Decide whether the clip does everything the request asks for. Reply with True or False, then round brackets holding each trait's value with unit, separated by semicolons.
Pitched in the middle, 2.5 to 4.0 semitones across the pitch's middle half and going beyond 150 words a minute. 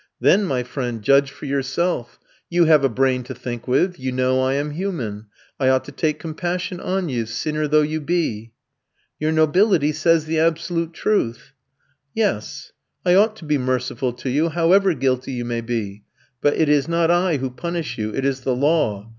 False (145 Hz; 4.7 semitones; 190 wpm)